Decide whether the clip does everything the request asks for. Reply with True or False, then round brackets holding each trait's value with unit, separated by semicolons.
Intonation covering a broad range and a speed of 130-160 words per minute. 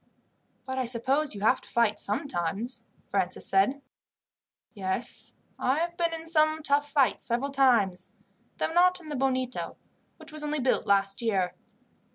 True (6.3 semitones; 155 wpm)